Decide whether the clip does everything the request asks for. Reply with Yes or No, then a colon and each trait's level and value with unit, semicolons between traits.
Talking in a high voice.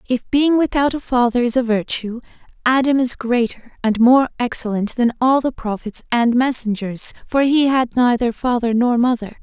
Yes: high, 245 Hz